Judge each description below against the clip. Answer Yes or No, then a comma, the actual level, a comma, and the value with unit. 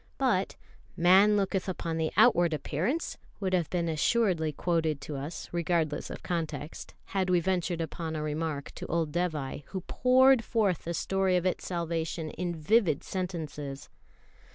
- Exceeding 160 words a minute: No, average, 155 wpm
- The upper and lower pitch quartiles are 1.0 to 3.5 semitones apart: Yes, average, 3.0 semitones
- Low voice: No, medium, 170 Hz